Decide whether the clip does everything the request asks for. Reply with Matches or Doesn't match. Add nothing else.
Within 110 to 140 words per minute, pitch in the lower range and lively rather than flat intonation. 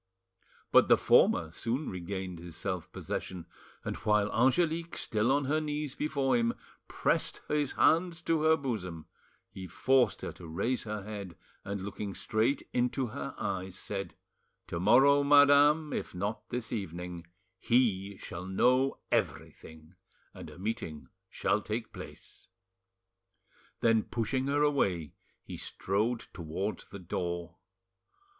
Matches